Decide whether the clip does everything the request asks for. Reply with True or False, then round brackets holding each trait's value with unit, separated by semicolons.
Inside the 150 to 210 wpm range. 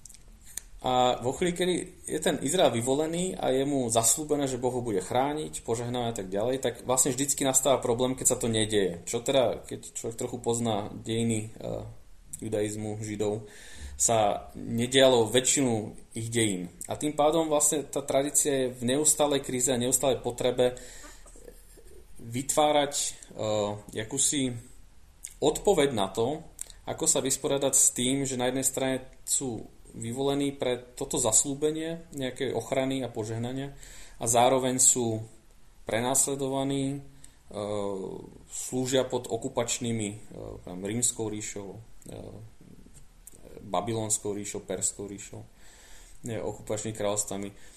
False (125 wpm)